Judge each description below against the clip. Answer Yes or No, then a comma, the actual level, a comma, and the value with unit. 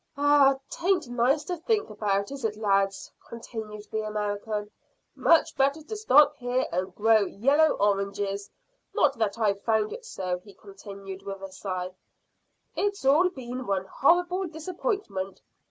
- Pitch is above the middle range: Yes, high, 220 Hz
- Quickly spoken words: No, average, 145 wpm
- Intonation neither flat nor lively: No, wide, 6.7 semitones